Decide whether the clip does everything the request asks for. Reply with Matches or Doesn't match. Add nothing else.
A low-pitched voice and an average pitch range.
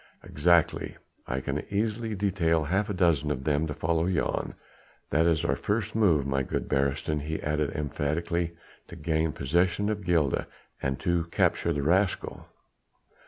Matches